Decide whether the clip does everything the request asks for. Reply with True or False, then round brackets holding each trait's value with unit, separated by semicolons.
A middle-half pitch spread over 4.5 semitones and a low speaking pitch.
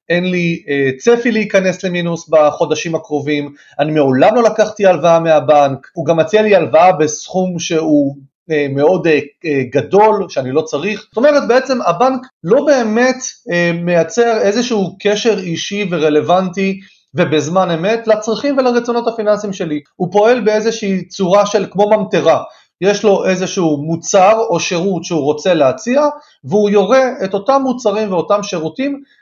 False (5.2 semitones; 190 Hz)